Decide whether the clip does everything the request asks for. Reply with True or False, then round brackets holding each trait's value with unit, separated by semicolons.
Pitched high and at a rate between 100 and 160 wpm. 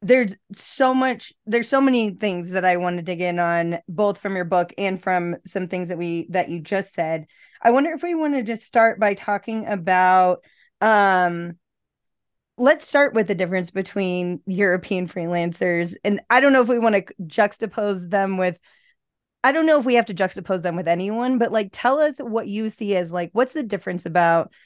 False (195 Hz; 200 wpm)